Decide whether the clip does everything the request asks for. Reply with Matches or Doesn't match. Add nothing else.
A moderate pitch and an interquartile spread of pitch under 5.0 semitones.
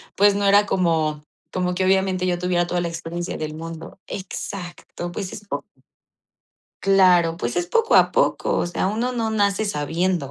Matches